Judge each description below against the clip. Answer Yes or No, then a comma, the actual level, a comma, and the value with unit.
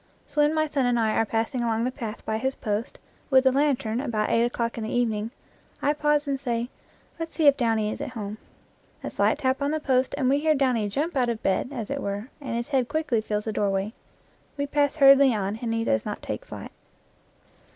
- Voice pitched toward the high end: Yes, high, 245 Hz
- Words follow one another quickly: Yes, fast, 230 wpm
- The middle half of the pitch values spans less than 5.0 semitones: Yes, average, 4.1 semitones